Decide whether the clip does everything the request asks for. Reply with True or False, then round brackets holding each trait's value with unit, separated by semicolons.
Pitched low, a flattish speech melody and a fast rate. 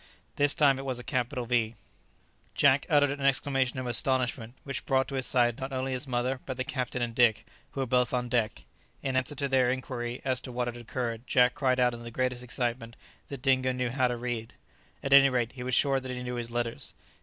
True (125 Hz; 1.6 semitones; 230 wpm)